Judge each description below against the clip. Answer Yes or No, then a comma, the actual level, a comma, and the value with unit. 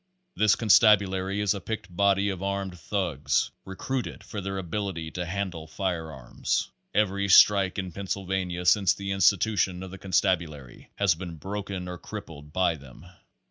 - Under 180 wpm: Yes, average, 155 wpm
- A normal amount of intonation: No, narrow, 2.2 semitones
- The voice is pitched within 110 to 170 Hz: No, very low, 95 Hz